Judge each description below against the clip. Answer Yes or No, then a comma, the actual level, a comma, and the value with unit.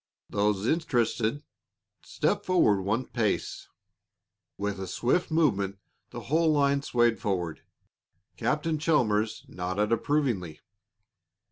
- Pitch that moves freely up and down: Yes, wide, 6.7 semitones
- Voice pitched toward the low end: Yes, low, 115 Hz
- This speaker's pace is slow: Yes, slow, 100 wpm